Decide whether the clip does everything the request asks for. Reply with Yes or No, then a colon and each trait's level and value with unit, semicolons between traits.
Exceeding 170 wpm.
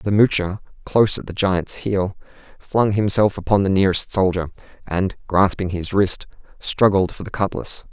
No: average, 160 wpm